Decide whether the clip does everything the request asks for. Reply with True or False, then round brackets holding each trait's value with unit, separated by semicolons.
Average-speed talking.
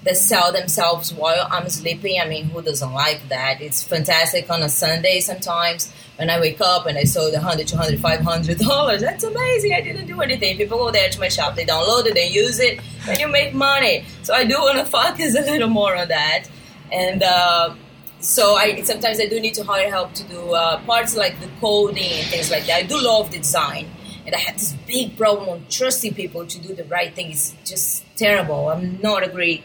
False (230 wpm)